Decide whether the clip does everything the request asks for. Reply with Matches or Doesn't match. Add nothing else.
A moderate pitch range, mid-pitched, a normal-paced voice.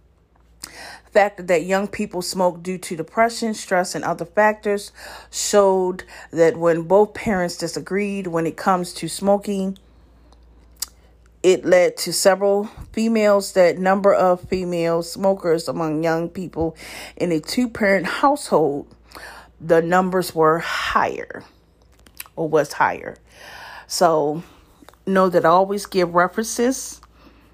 Doesn't match